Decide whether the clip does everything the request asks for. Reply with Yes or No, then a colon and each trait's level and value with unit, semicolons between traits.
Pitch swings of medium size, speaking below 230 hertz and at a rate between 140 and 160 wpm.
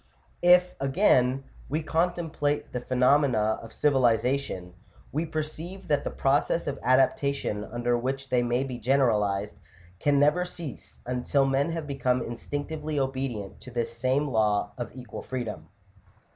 Yes: average, 3.5 semitones; low, 135 Hz; average, 150 wpm